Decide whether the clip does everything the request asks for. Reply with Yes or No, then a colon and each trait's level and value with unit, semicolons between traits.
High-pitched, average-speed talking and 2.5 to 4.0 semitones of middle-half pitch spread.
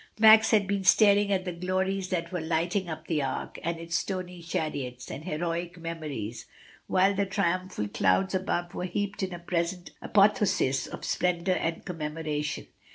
No: medium, 175 Hz; average, 160 wpm; average, 2.8 semitones